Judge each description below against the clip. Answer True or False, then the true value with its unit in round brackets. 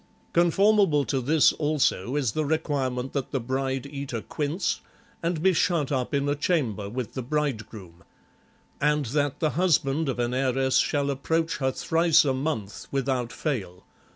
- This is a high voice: False (140 Hz)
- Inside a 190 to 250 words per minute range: False (165 wpm)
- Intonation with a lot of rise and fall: False (3.3 semitones)